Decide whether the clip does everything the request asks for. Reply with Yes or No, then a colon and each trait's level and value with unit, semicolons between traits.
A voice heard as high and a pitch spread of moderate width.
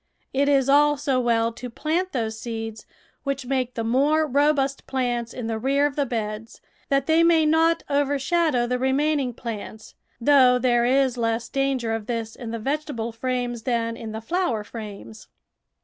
Yes: very high, 250 Hz; average, 3.6 semitones